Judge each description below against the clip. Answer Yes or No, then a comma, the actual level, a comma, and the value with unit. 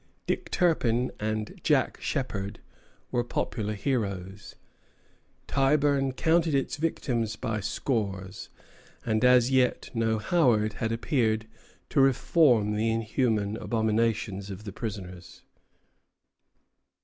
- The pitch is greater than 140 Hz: No, low, 115 Hz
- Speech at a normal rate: No, slow, 100 wpm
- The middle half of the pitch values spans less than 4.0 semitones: Yes, average, 3.6 semitones